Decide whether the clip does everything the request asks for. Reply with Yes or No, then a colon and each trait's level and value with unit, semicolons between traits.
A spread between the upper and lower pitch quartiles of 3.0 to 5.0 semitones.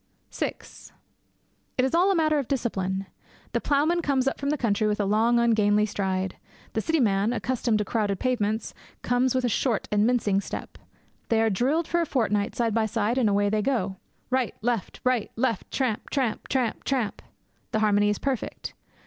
Yes: average, 3.9 semitones